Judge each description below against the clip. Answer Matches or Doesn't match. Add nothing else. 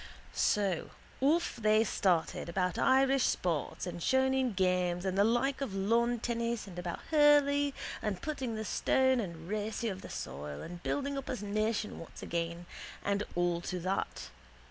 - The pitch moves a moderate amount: Doesn't match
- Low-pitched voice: Doesn't match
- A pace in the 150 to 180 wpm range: Matches